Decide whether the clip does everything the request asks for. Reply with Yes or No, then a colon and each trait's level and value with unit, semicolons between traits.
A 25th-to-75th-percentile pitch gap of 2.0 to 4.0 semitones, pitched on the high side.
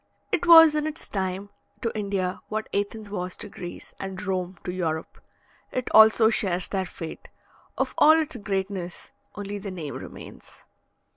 Yes: average, 3.0 semitones; high, 200 Hz